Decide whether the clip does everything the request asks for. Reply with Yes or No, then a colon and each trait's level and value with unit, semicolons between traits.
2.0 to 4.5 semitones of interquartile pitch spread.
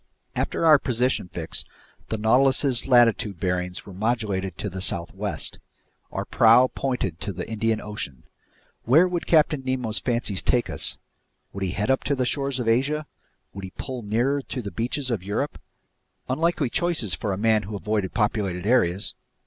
No: average, 4.9 semitones